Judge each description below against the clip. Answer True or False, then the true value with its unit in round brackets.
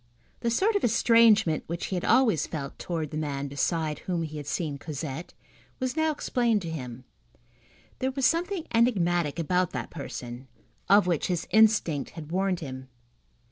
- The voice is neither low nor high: True (175 Hz)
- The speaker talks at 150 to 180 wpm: True (165 wpm)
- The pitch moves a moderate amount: False (7.2 semitones)